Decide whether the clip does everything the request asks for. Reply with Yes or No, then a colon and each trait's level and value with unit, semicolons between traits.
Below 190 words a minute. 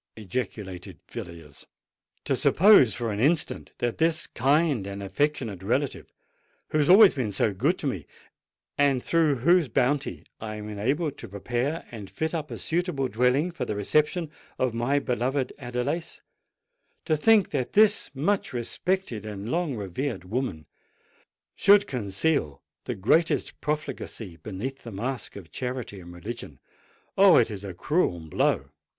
Yes: average, 140 wpm